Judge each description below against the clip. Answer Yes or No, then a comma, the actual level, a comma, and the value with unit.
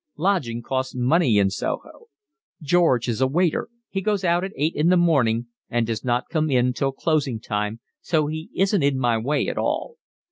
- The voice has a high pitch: No, medium, 140 Hz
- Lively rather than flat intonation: Yes, wide, 6.0 semitones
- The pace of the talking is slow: No, average, 190 wpm